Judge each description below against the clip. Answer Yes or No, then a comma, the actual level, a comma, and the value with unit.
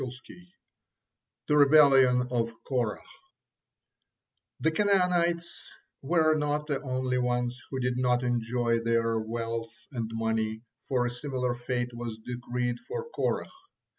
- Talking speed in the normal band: No, slow, 115 wpm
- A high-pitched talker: No, low, 125 Hz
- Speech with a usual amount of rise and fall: Yes, average, 3.4 semitones